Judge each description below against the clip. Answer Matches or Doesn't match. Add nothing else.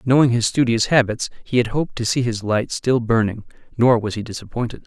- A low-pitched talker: Matches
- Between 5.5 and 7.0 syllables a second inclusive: Matches